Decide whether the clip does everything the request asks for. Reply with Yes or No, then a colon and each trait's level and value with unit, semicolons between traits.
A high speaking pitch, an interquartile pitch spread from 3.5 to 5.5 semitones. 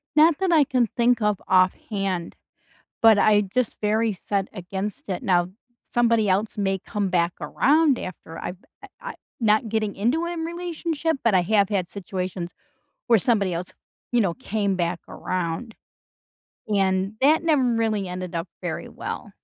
Yes: high, 205 Hz; average, 4.4 semitones